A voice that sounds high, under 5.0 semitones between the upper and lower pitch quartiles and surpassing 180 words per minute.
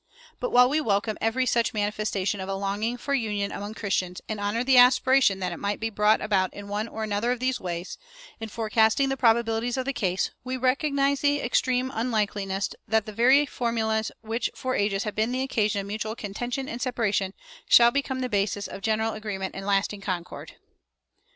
Yes: high, 220 Hz; average, 3.5 semitones; average, 195 wpm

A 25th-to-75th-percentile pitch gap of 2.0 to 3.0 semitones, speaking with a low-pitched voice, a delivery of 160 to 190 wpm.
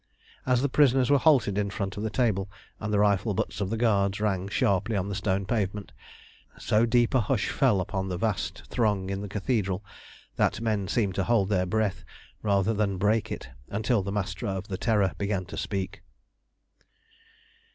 Yes: narrow, 2.5 semitones; low, 100 Hz; average, 185 wpm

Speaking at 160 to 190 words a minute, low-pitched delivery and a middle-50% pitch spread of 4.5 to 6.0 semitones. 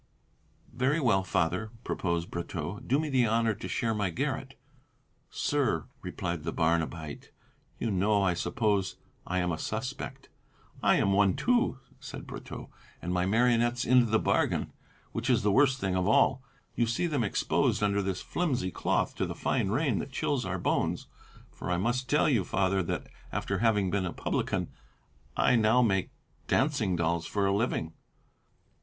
Yes: average, 165 wpm; low, 100 Hz; average, 4.9 semitones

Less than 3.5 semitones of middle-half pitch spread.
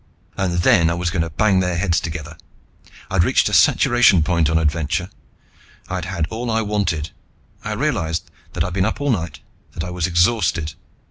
Yes: average, 2.7 semitones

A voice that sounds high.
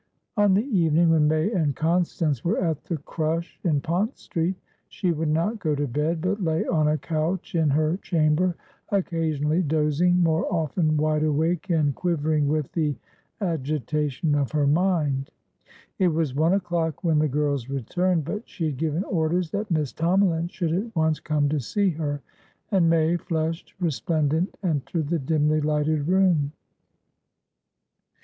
No: medium, 160 Hz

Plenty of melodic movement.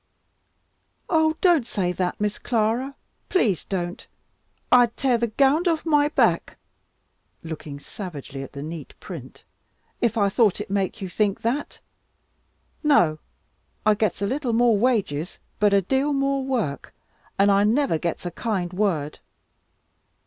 Yes: wide, 6.8 semitones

